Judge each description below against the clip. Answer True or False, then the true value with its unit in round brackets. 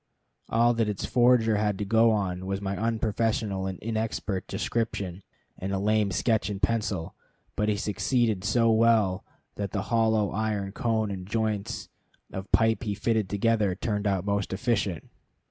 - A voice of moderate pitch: False (105 Hz)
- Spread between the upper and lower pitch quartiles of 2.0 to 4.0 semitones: True (2.4 semitones)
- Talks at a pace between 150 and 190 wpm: True (160 wpm)